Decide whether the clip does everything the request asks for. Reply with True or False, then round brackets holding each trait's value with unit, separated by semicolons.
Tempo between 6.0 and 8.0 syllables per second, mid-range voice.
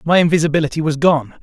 True (6.9 syllables/s; 155 Hz)